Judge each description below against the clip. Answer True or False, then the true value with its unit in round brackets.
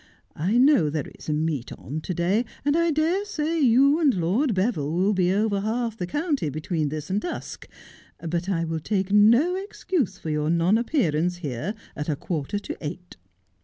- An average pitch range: False (8.2 semitones)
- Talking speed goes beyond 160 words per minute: True (190 wpm)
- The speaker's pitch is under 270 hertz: True (190 Hz)